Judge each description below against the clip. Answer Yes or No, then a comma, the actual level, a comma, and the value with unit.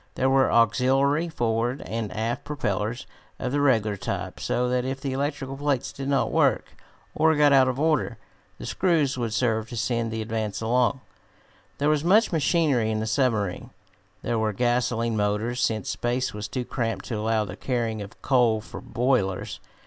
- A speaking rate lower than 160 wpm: No, average, 175 wpm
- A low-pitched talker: Yes, low, 120 Hz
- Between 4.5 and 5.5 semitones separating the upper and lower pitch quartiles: No, average, 3.5 semitones